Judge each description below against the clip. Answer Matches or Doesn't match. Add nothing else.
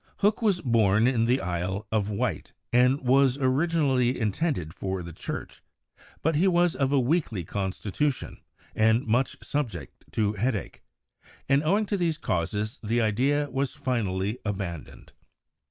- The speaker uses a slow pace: Doesn't match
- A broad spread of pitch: Matches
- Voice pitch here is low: Matches